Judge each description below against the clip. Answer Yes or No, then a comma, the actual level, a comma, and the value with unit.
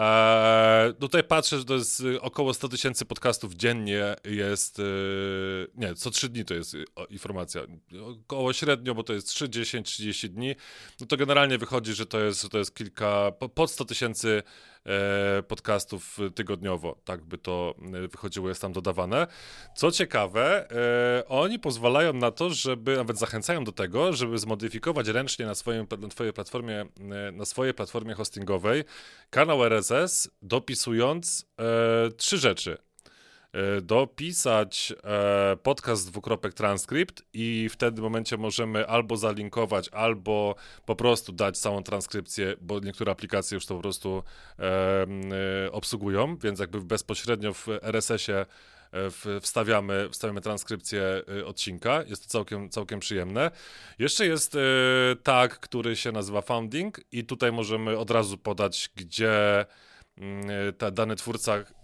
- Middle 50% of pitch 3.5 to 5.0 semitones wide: No, average, 3.1 semitones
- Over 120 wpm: Yes, average, 130 wpm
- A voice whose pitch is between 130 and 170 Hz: No, low, 110 Hz